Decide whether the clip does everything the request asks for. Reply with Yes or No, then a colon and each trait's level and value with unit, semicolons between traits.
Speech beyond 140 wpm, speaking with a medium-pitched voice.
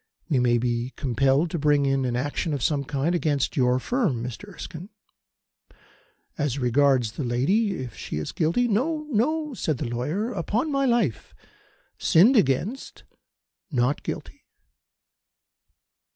No: slow, 135 wpm; medium, 145 Hz